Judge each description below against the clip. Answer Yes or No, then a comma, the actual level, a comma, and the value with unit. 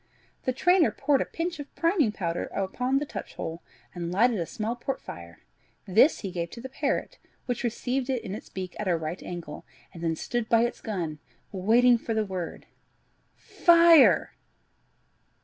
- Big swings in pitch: Yes, wide, 6.7 semitones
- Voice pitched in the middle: No, high, 225 Hz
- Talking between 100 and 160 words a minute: No, average, 175 wpm